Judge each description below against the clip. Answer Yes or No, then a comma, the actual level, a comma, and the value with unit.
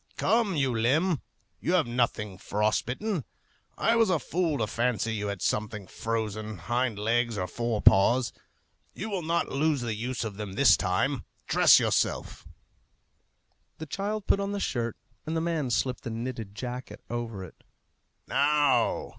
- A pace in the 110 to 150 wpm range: No, average, 160 wpm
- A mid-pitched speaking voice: No, low, 120 Hz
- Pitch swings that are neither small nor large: No, wide, 6.5 semitones